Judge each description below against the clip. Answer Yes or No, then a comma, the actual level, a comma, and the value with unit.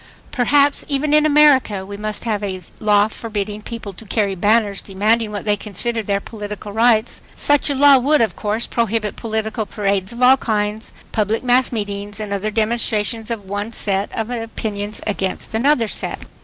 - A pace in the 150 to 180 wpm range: Yes, average, 170 wpm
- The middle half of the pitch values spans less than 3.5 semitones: Yes, narrow, 2.4 semitones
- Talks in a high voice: Yes, high, 215 Hz